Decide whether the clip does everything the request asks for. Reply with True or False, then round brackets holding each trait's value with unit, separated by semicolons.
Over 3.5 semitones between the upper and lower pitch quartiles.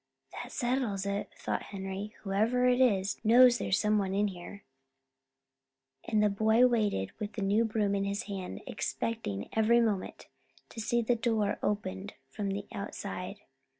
False (2.6 semitones)